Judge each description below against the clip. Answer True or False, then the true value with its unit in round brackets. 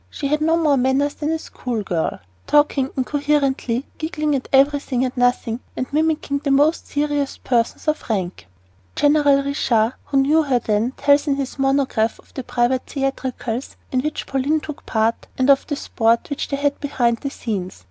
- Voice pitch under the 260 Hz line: False (275 Hz)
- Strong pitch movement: False (2.8 semitones)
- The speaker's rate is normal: True (180 wpm)